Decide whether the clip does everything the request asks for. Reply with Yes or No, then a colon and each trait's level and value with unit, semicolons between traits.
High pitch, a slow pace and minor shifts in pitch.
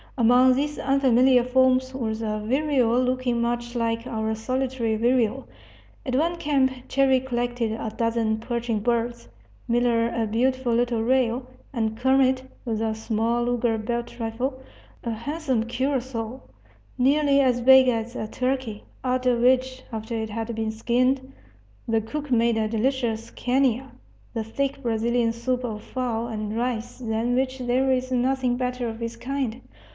No: high, 245 Hz; average, 150 wpm; narrow, 2.3 semitones